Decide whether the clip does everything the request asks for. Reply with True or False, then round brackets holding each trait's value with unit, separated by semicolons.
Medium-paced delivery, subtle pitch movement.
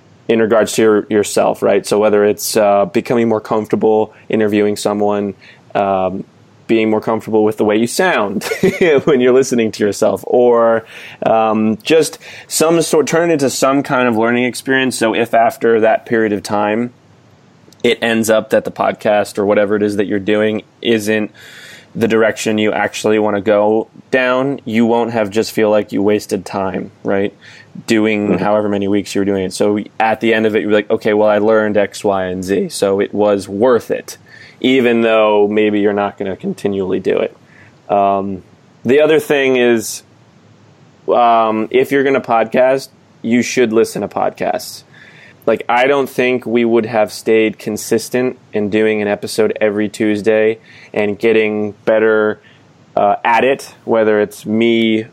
True (175 wpm; 2.0 semitones)